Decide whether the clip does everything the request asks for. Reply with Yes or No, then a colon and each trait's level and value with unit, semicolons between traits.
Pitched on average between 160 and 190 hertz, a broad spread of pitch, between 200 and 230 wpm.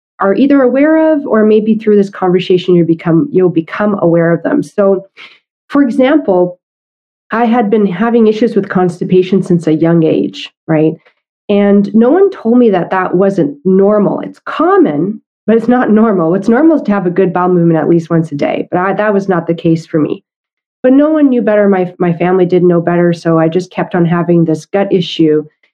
No: medium, 185 Hz; average, 4.5 semitones; fast, 205 wpm